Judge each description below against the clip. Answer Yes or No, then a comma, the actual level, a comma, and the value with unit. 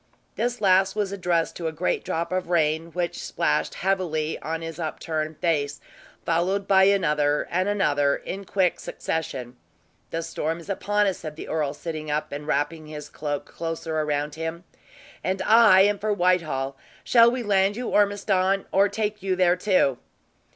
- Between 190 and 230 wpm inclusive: No, average, 165 wpm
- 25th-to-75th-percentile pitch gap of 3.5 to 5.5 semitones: Yes, average, 4.0 semitones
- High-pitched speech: No, medium, 170 Hz